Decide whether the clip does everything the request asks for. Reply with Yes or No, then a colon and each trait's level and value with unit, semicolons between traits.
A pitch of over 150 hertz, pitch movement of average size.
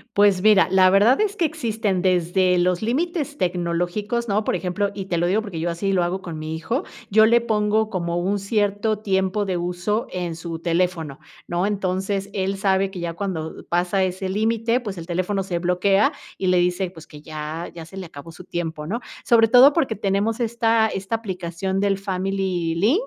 Yes: high, 190 Hz; average, 3.2 semitones